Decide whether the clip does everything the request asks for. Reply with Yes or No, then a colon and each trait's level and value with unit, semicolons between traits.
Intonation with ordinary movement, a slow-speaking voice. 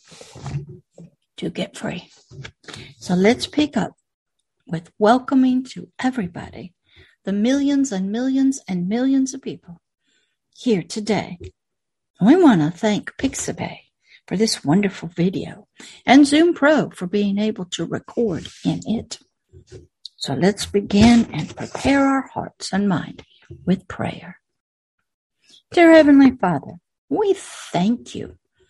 No: wide, 6.7 semitones; slow, 120 wpm